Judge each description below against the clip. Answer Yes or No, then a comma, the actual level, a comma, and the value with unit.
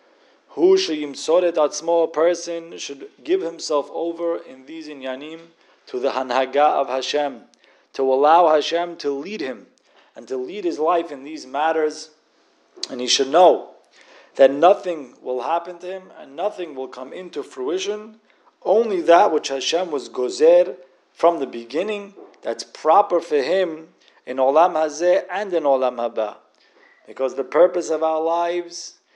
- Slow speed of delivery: No, average, 150 wpm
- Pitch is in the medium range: Yes, medium, 165 Hz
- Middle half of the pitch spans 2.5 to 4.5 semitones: No, average, 5.1 semitones